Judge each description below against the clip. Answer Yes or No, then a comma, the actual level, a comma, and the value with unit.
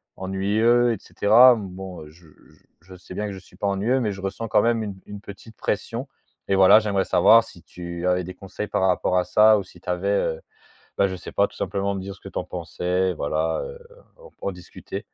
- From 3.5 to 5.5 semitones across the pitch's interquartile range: No, average, 2.8 semitones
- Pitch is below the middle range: Yes, low, 100 Hz